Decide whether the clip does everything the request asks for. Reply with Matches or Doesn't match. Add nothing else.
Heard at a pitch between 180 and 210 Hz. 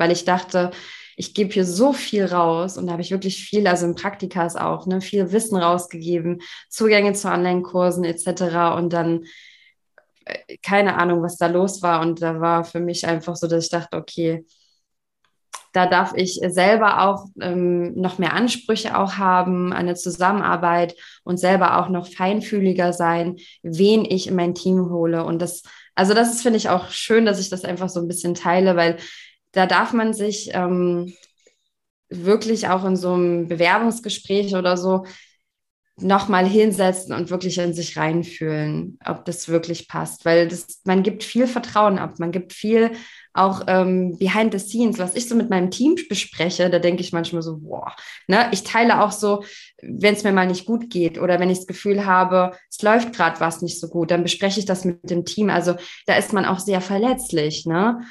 Matches